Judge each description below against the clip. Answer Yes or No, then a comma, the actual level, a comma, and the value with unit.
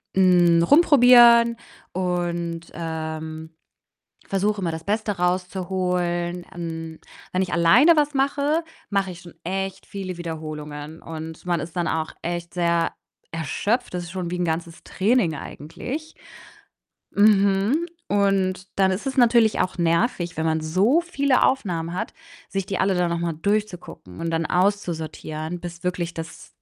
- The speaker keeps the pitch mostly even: No, average, 3.3 semitones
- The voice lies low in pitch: No, medium, 180 Hz